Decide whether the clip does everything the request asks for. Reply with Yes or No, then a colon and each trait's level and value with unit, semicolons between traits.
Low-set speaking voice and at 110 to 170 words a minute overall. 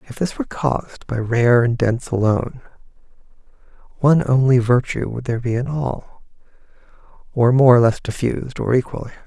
Yes: low, 125 Hz; average, 155 wpm